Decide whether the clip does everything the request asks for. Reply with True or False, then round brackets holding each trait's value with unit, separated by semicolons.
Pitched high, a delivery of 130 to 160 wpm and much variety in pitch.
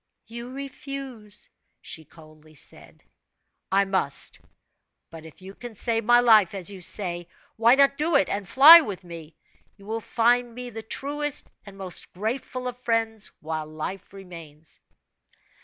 True (210 Hz; 150 wpm; 5.7 semitones)